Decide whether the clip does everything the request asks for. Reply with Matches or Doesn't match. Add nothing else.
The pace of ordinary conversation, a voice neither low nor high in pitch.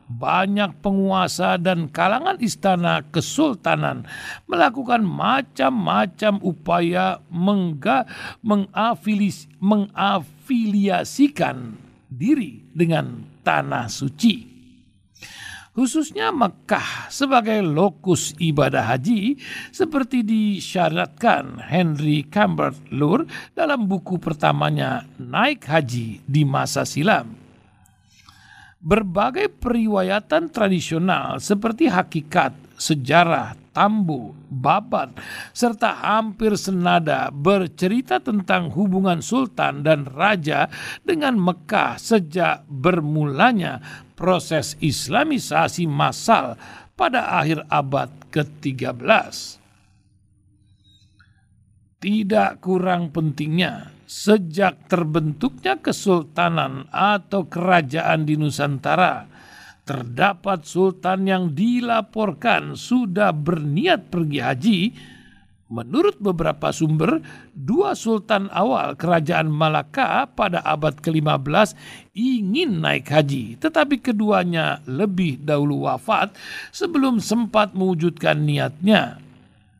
Doesn't match